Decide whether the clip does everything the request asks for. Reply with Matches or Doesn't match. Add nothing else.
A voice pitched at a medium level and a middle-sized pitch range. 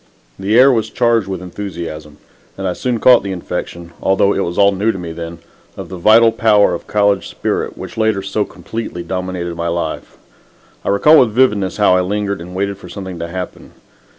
Doesn't match